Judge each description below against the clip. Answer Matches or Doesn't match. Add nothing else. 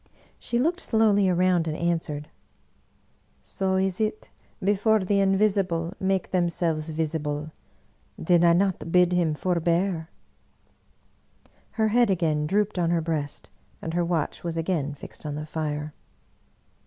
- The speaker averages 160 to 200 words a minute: Doesn't match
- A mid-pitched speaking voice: Matches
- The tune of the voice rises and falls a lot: Doesn't match